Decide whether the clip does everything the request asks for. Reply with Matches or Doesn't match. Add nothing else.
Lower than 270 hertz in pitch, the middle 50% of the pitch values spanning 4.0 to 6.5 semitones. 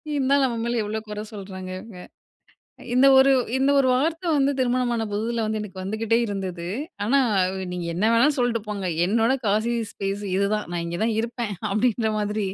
Doesn't match